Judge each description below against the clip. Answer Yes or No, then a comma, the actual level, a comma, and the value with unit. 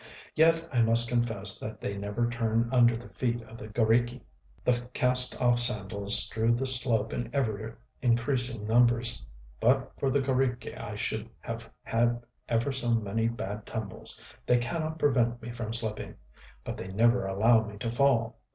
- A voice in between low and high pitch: No, low, 115 Hz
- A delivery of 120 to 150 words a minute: No, average, 165 wpm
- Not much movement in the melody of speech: Yes, narrow, 1.8 semitones